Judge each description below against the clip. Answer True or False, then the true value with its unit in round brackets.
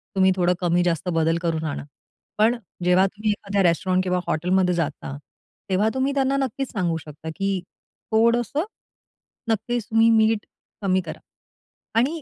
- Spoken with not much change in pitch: False (4.3 semitones)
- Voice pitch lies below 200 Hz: True (190 Hz)